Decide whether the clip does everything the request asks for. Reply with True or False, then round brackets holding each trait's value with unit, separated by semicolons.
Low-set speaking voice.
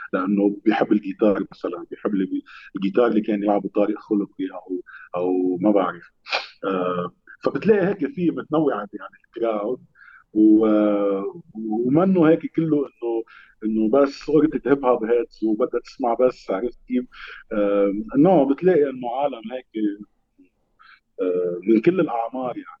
True (110 Hz)